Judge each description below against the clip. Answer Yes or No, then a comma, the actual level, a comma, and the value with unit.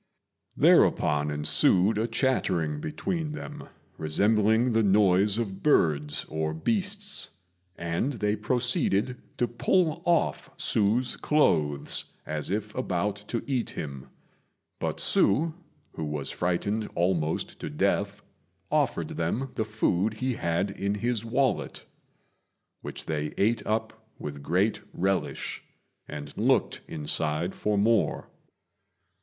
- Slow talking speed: Yes, slow, 115 wpm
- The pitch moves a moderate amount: No, wide, 6.4 semitones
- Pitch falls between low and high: No, low, 105 Hz